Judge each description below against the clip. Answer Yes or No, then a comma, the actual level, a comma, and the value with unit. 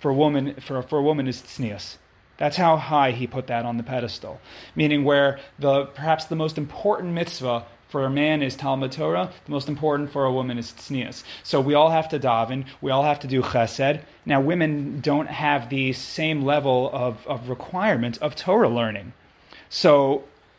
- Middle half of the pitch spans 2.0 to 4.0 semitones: Yes, narrow, 2.6 semitones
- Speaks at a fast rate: No, average, 195 wpm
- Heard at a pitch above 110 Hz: Yes, medium, 140 Hz